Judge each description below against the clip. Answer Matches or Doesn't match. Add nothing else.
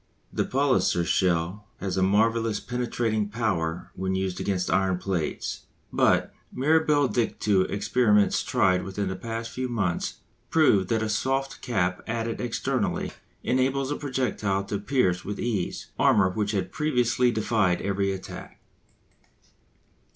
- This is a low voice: Matches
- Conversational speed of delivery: Doesn't match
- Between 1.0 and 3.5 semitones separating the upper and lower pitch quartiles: Doesn't match